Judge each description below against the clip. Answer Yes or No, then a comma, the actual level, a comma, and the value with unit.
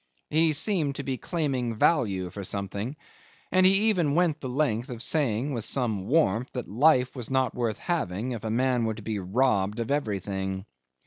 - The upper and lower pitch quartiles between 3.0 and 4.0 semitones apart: No, wide, 5.4 semitones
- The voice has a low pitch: Yes, low, 125 Hz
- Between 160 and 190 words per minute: Yes, average, 185 wpm